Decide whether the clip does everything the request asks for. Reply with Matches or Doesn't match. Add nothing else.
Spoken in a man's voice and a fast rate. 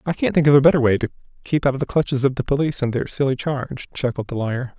Matches